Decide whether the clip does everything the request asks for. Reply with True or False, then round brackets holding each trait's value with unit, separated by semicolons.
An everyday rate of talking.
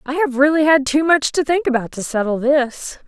False (235 wpm)